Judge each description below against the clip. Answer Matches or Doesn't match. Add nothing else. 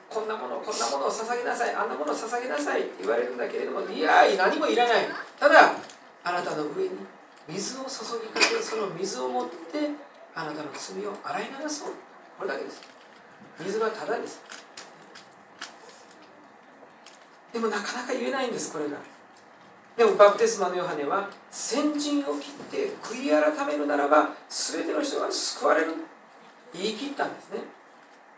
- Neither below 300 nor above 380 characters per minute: Matches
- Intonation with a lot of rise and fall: Matches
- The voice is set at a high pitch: Matches